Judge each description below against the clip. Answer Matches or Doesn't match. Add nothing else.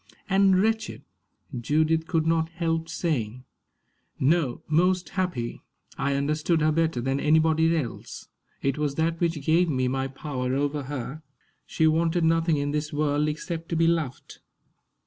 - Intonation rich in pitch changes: Doesn't match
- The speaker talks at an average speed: Matches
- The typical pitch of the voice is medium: Matches